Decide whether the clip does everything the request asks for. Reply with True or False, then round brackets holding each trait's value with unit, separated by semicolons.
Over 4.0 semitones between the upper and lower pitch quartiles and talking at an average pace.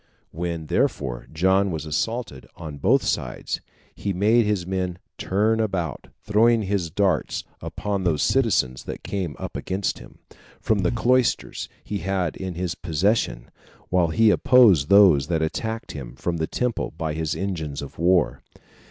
True (4.6 semitones; 150 wpm)